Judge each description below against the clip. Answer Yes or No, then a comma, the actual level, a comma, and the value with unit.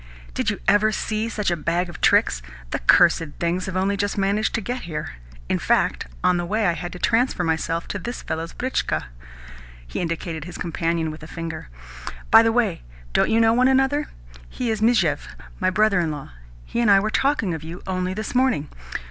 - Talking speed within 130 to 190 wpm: No, fast, 205 wpm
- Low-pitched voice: No, medium, 185 Hz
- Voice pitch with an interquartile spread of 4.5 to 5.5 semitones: Yes, average, 5.0 semitones